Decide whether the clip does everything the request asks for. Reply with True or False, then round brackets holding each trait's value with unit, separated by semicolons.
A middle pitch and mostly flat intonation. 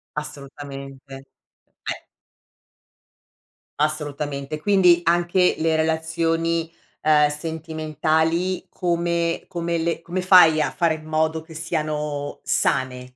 True (160 Hz; 2.1 semitones)